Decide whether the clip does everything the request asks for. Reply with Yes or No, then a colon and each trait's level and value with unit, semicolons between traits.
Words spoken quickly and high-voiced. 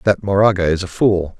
No: fast, 215 wpm; very low, 95 Hz